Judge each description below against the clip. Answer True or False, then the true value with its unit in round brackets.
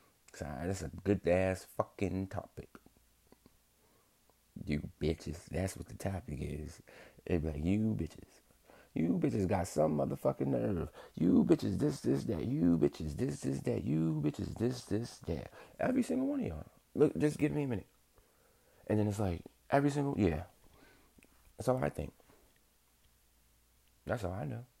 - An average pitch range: False (6.0 semitones)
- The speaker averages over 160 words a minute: False (155 wpm)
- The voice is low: True (90 Hz)